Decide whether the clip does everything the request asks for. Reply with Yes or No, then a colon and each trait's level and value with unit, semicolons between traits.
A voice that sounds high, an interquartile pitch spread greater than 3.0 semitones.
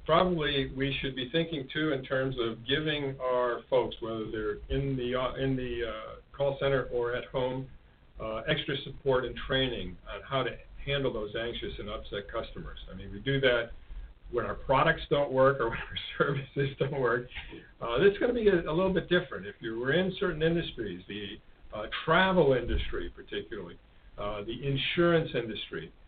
No: low, 135 Hz; average, 4.2 semitones